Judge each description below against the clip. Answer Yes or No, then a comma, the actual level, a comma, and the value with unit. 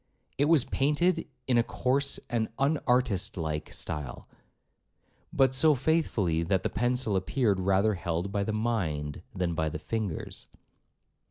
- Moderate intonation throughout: No, wide, 6.6 semitones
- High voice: No, low, 110 Hz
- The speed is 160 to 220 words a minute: No, average, 140 wpm